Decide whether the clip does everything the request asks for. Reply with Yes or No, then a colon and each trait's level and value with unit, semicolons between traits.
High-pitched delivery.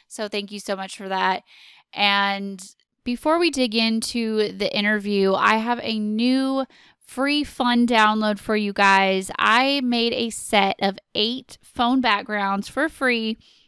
Yes: high, 215 Hz